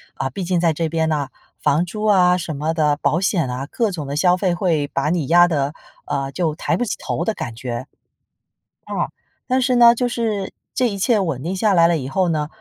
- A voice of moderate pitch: Yes, medium, 170 Hz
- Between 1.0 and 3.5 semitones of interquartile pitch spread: No, average, 4.5 semitones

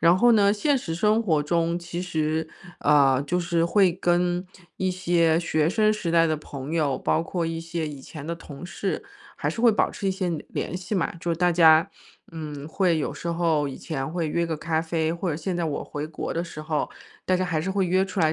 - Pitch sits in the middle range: Yes, medium, 170 Hz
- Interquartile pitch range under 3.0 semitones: Yes, narrow, 2.5 semitones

